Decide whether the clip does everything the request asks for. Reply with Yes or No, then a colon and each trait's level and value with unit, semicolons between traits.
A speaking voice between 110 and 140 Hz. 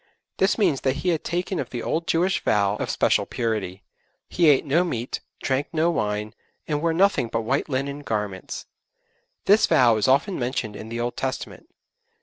Yes: low, 135 Hz